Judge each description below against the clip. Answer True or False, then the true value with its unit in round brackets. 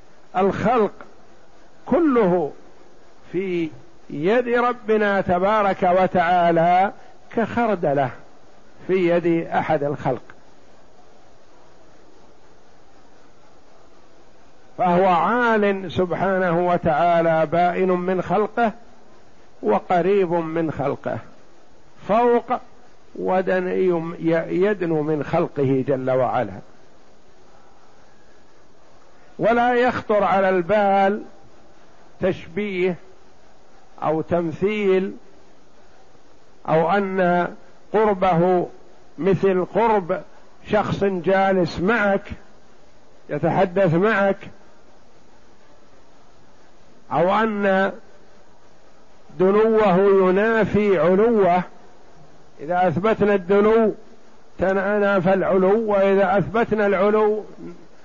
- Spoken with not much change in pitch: False (3.0 semitones)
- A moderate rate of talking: False (60 wpm)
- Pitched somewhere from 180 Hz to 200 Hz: True (190 Hz)